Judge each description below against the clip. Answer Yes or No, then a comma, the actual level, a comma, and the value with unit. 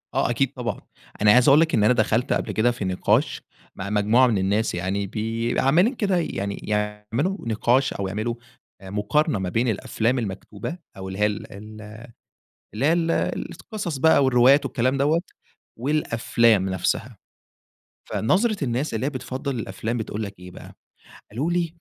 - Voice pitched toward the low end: Yes, low, 115 Hz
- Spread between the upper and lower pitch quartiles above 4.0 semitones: Yes, average, 4.7 semitones